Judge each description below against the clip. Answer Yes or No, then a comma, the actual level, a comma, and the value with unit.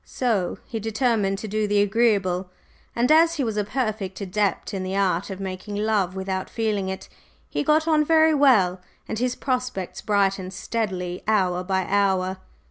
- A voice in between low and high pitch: No, high, 205 Hz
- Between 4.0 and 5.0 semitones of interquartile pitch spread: No, average, 3.5 semitones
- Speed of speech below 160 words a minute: No, average, 170 wpm